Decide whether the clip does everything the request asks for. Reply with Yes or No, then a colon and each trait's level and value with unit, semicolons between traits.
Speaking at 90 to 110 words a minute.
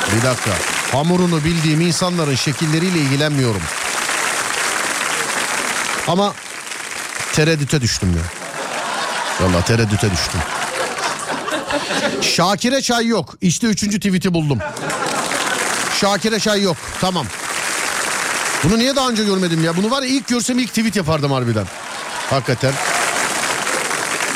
Yes: average, 100 wpm